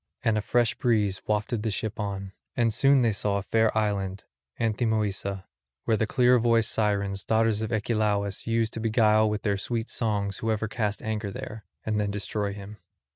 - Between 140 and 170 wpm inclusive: No, average, 180 wpm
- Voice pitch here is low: Yes, low, 110 Hz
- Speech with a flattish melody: Yes, narrow, 1.9 semitones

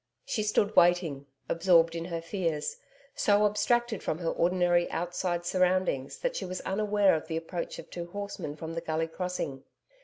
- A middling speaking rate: Yes, average, 165 wpm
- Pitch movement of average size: Yes, average, 3.1 semitones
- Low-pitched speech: No, medium, 175 Hz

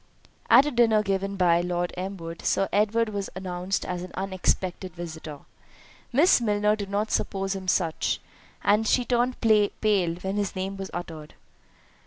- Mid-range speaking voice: No, high, 195 Hz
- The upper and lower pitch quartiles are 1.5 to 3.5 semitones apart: Yes, average, 2.9 semitones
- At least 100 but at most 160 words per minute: Yes, average, 155 wpm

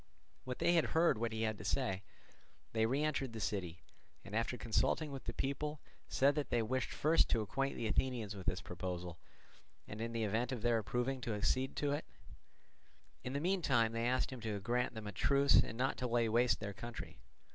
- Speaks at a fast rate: Yes, fast, 210 wpm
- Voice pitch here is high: No, low, 120 Hz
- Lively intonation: No, average, 3.6 semitones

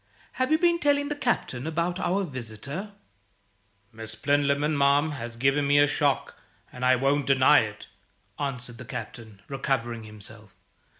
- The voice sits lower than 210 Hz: Yes, medium, 140 Hz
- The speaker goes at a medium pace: Yes, average, 145 wpm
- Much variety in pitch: No, average, 4.7 semitones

